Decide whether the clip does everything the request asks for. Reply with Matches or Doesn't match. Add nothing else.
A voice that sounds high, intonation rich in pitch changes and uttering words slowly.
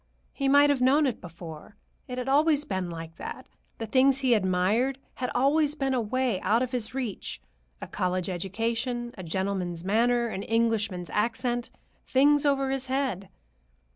Doesn't match